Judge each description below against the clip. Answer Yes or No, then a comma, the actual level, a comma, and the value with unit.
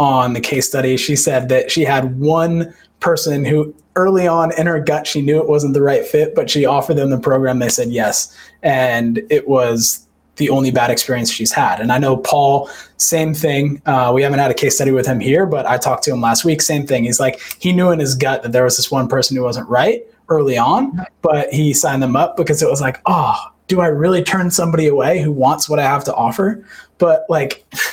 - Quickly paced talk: Yes, fast, 235 wpm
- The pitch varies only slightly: No, average, 4.2 semitones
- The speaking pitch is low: No, medium, 145 Hz